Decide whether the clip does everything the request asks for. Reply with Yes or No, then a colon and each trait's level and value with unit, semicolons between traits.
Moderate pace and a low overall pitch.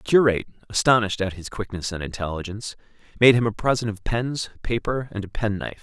Yes: average, 185 wpm; low, 105 Hz